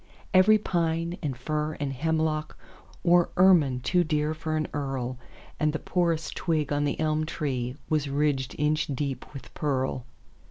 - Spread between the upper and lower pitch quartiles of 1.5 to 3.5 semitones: Yes, average, 2.8 semitones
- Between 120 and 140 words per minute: Yes, slow, 135 wpm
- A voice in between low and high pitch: Yes, medium, 150 Hz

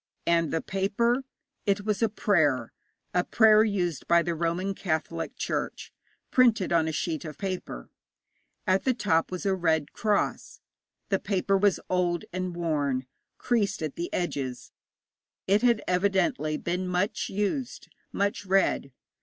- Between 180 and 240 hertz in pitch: Yes, medium, 185 Hz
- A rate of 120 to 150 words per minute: Yes, average, 145 wpm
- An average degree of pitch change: Yes, average, 3.6 semitones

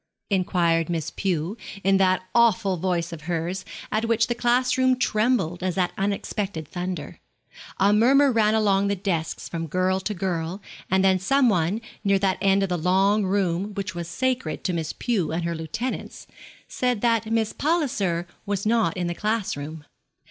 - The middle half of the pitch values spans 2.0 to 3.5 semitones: No, average, 4.1 semitones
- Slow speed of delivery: No, average, 175 wpm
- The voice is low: No, high, 195 Hz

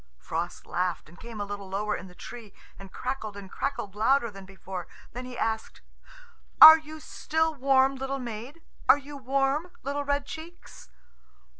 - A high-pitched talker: Yes, very high, 250 Hz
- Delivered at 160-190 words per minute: Yes, average, 165 wpm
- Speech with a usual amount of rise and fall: No, wide, 5.8 semitones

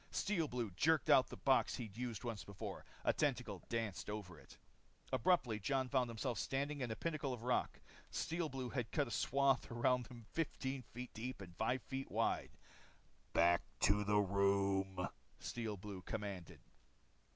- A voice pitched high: No, low, 120 Hz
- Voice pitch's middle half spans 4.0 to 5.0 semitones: Yes, average, 4.7 semitones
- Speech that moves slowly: No, average, 160 wpm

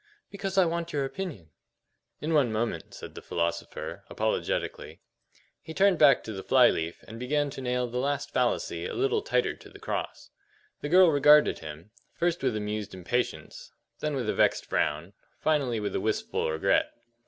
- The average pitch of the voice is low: Yes, low, 130 Hz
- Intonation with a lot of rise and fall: Yes, wide, 6.7 semitones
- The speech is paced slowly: No, average, 175 wpm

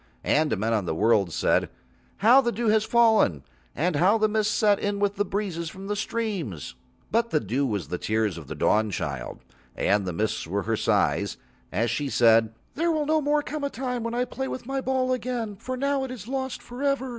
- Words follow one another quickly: Yes, fast, 215 wpm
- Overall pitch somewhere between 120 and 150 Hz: No, high, 205 Hz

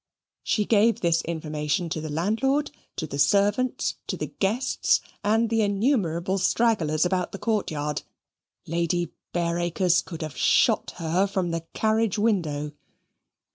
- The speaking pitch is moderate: Yes, medium, 180 Hz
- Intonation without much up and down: No, average, 4.7 semitones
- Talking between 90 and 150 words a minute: Yes, slow, 135 wpm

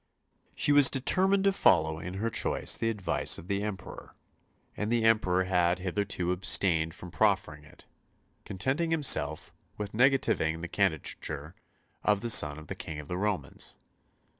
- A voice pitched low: Yes, very low, 95 Hz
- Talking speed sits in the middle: Yes, average, 155 wpm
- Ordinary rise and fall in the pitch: No, wide, 5.7 semitones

